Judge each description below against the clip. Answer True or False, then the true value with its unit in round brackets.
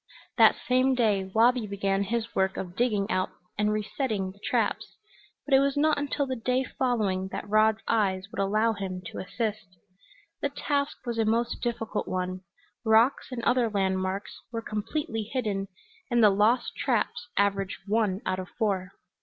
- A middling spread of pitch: True (3.6 semitones)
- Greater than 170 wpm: False (165 wpm)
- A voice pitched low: False (215 Hz)